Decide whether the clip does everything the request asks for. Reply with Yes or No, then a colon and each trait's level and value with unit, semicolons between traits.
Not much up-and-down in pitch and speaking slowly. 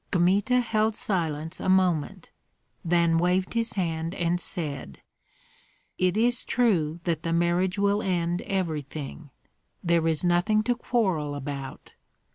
No: average, 3.6 semitones; slow, 125 wpm